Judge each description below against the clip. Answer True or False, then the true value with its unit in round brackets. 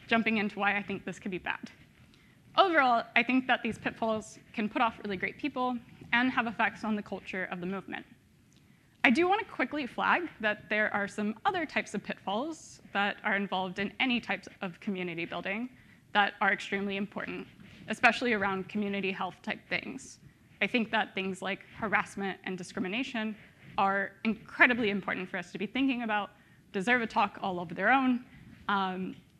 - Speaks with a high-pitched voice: True (210 Hz)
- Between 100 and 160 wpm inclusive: False (180 wpm)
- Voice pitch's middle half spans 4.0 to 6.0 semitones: False (3.3 semitones)